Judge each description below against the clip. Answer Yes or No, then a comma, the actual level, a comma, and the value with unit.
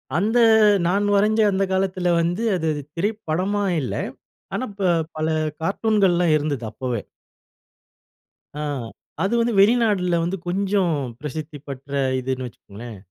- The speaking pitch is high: No, medium, 180 Hz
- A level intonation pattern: No, average, 4.9 semitones